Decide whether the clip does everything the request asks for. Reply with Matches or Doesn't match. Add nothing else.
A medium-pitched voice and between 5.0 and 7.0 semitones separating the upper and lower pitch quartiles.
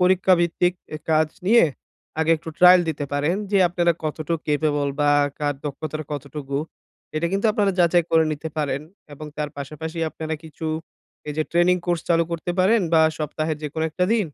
Doesn't match